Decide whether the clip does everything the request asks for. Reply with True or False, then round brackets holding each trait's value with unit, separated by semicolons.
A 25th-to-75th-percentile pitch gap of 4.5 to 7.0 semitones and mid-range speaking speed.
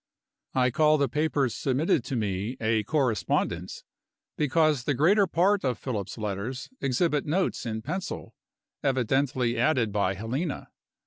False (5.1 semitones; 130 wpm)